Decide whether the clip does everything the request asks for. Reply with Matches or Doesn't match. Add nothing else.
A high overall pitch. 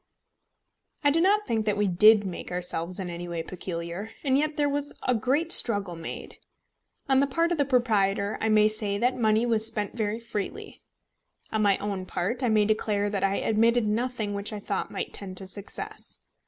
Matches